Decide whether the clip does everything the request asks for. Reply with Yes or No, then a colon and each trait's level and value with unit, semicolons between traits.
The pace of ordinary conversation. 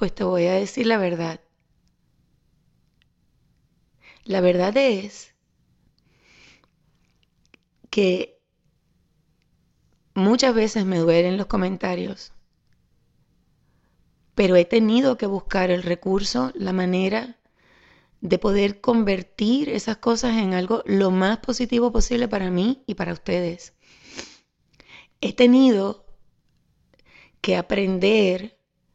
No: slow, 95 wpm